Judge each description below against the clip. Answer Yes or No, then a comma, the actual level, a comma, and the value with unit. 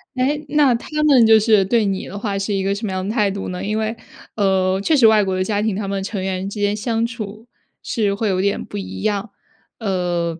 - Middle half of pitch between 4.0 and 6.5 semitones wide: No, narrow, 2.6 semitones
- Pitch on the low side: No, high, 205 Hz